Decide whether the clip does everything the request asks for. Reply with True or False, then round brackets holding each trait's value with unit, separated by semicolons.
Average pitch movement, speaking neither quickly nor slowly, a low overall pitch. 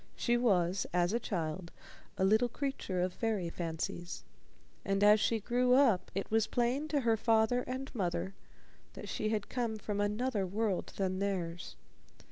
False (4.4 semitones; 160 wpm; 210 Hz)